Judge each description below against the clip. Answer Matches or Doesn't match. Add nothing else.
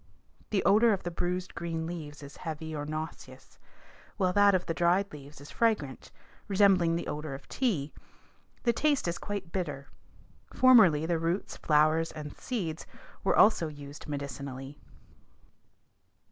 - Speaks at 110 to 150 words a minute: Matches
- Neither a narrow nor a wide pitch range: Matches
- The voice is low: Doesn't match